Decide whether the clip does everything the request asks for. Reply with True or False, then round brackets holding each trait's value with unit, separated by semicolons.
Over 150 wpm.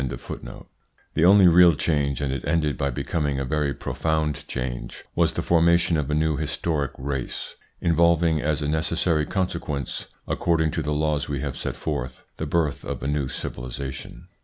True (170 wpm)